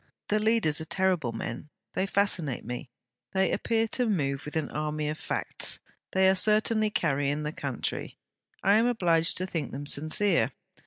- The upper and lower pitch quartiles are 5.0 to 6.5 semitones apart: Yes, wide, 5.6 semitones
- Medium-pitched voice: Yes, medium, 165 Hz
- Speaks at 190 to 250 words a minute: No, average, 165 wpm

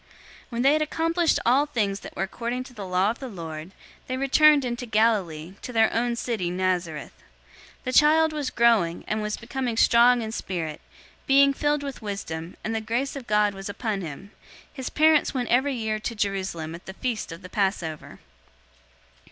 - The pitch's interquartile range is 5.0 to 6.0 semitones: Yes, average, 5.3 semitones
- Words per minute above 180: Yes, average, 195 wpm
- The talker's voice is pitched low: No, high, 225 Hz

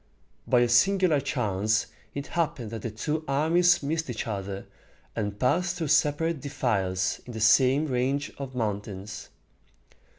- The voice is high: No, low, 130 Hz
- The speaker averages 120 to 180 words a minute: Yes, average, 140 wpm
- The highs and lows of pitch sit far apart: Yes, wide, 6.0 semitones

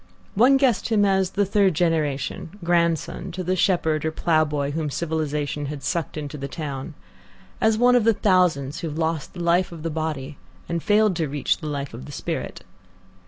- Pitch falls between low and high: Yes, medium, 165 Hz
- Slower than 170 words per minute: No, average, 190 wpm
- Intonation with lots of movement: No, average, 4.0 semitones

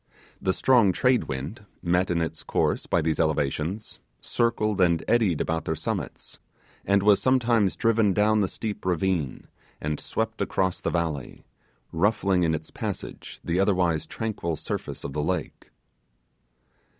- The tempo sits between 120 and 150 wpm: Yes, average, 145 wpm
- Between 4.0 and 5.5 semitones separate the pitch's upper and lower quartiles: Yes, average, 4.6 semitones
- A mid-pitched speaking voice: No, very low, 90 Hz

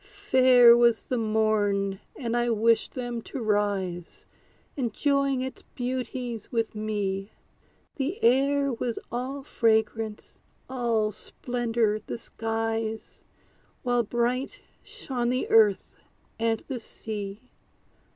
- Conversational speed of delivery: No, slow, 105 wpm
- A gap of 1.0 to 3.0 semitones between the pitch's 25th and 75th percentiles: Yes, average, 2.7 semitones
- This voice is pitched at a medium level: No, high, 230 Hz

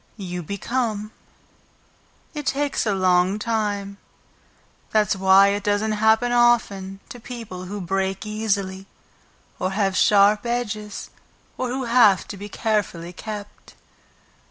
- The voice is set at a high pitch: Yes, high, 205 Hz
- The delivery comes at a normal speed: No, slow, 120 wpm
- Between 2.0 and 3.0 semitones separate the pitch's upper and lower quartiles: Yes, narrow, 2.5 semitones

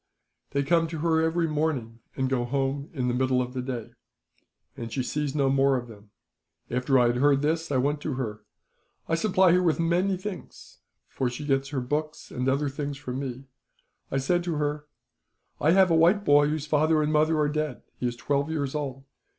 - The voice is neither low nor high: Yes, medium, 145 Hz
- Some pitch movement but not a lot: Yes, average, 3.3 semitones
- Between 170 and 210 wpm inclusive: Yes, fast, 205 wpm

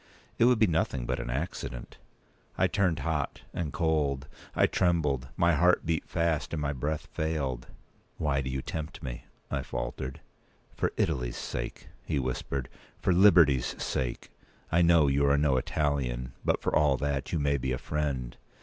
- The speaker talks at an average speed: Yes, average, 170 wpm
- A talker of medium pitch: No, very low, 70 Hz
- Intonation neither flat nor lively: Yes, average, 3.7 semitones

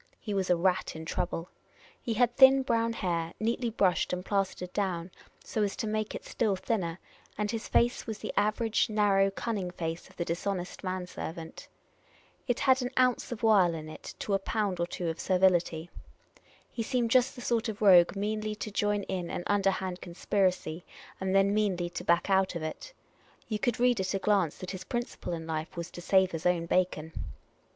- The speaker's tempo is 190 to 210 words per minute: Yes, average, 195 wpm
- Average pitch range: Yes, average, 3.6 semitones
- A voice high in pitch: Yes, high, 195 Hz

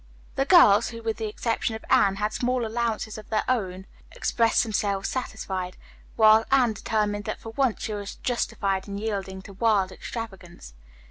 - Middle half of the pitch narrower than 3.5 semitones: Yes, narrow, 2.5 semitones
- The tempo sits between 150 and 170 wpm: Yes, average, 165 wpm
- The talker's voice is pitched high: Yes, high, 215 Hz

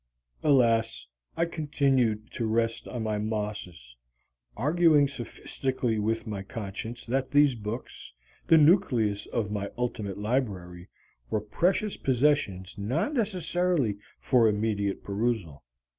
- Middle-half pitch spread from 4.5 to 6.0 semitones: Yes, average, 5.2 semitones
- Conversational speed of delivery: No, slow, 115 wpm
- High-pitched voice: No, low, 115 Hz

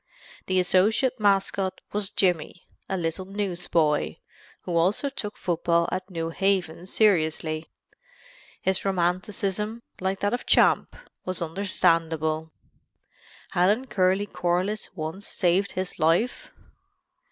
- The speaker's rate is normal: No, slow, 105 wpm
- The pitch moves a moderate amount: Yes, average, 3.0 semitones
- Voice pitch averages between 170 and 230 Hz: Yes, medium, 185 Hz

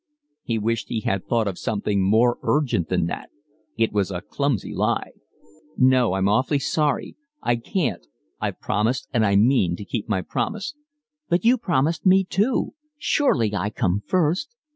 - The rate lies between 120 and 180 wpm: Yes, average, 160 wpm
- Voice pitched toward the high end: No, low, 115 Hz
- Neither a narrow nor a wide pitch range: No, wide, 7.0 semitones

